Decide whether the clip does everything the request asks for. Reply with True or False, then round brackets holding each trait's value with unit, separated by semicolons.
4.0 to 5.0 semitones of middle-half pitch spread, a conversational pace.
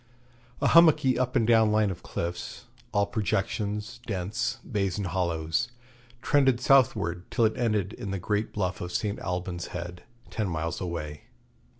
True (4.4 semitones; 155 wpm)